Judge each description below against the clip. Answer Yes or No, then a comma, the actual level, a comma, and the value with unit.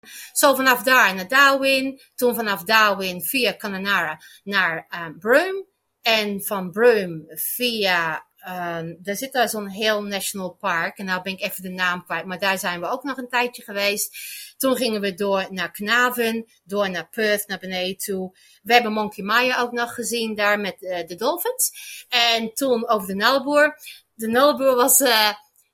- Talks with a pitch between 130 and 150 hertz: No, high, 215 Hz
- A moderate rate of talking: Yes, average, 175 wpm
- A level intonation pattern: No, average, 4.3 semitones